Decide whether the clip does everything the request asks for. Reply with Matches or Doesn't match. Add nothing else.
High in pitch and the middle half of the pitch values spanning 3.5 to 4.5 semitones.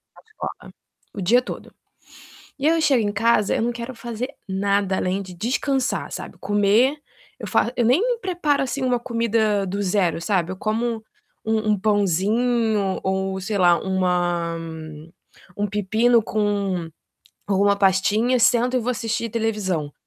Matches